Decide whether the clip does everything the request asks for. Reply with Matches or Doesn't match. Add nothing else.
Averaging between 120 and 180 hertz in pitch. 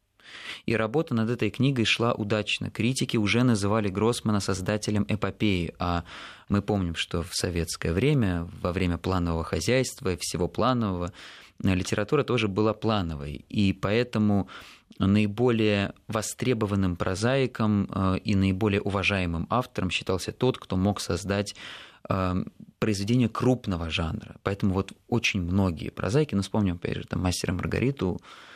Doesn't match